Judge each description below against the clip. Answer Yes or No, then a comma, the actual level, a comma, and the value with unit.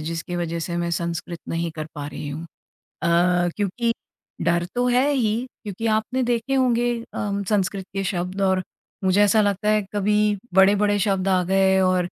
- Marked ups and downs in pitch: No, average, 3.6 semitones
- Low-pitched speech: No, high, 195 Hz